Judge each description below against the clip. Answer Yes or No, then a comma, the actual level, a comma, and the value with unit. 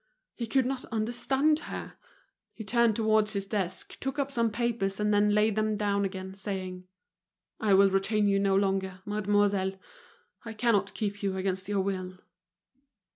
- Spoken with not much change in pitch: Yes, narrow, 2.3 semitones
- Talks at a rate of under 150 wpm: No, average, 160 wpm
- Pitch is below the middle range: No, high, 205 Hz